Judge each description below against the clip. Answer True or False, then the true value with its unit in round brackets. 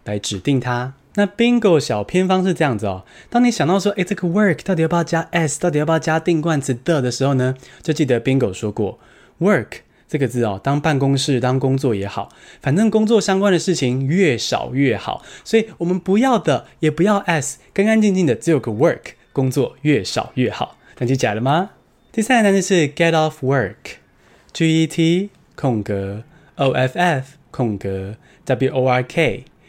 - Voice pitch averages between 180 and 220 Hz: False (155 Hz)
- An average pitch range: False (6.0 semitones)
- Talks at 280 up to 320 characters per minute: True (315 characters per minute)